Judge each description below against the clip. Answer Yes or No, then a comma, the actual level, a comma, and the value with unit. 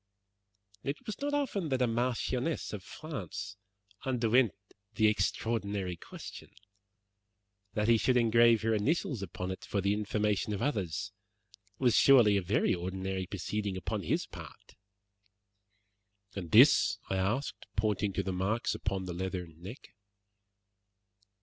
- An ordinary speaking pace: No, slow, 130 wpm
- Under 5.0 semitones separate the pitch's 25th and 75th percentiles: Yes, average, 4.2 semitones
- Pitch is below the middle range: Yes, low, 105 Hz